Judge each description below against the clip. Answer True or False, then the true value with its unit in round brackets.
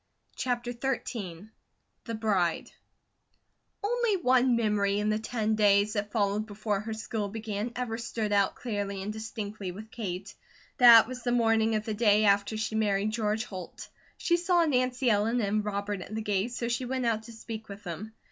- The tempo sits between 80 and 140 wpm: False (175 wpm)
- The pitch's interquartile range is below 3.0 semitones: True (2.5 semitones)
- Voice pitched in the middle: False (220 Hz)